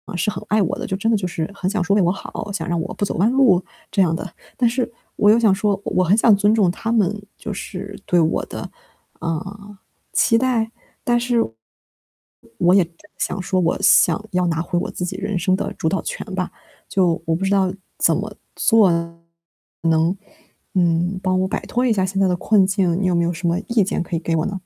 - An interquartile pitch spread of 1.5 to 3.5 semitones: Yes, average, 2.9 semitones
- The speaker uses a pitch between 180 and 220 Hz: Yes, high, 190 Hz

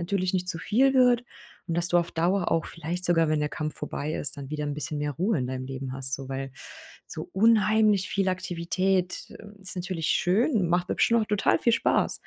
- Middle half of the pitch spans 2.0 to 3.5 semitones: No, average, 4.6 semitones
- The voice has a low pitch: No, medium, 175 Hz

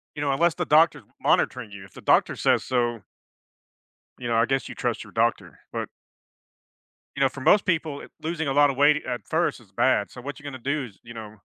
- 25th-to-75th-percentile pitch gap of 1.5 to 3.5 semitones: No, average, 4.1 semitones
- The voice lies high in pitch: No, low, 135 Hz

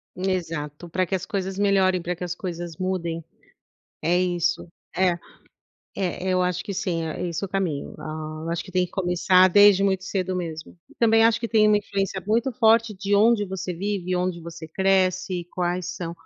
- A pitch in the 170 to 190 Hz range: Yes, medium, 185 Hz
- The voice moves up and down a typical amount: No, narrow, 2.2 semitones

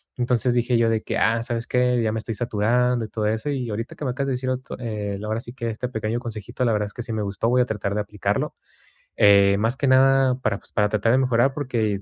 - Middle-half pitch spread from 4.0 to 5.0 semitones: No, narrow, 2.6 semitones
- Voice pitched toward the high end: No, low, 115 Hz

